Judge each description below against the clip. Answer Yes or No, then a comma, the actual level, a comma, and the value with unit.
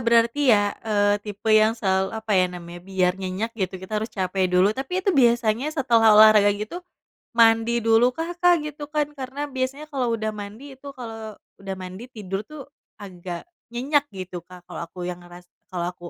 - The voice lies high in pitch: Yes, high, 215 Hz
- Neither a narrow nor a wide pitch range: Yes, average, 4.5 semitones